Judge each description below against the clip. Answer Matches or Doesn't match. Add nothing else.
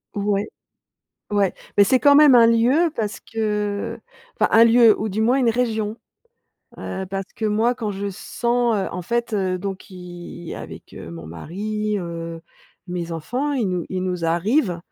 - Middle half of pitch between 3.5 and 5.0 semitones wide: Matches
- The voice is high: Matches